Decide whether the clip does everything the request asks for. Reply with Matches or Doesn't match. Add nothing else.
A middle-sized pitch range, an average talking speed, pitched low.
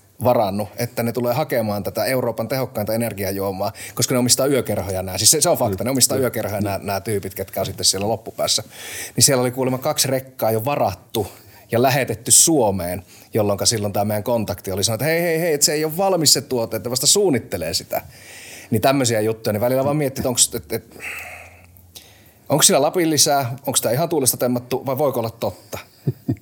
Doesn't match